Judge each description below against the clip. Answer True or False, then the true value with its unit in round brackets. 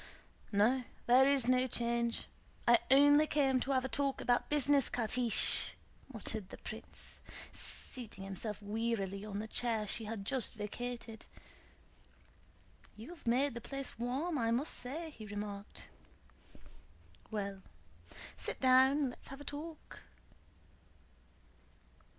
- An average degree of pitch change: True (3.8 semitones)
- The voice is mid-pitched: False (245 Hz)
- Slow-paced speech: True (125 wpm)